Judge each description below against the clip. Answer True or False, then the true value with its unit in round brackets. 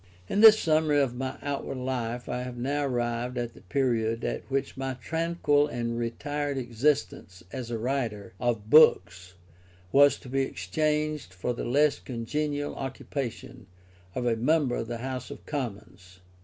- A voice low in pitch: True (125 Hz)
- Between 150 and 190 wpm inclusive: True (155 wpm)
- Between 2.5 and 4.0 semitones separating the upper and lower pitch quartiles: True (3.6 semitones)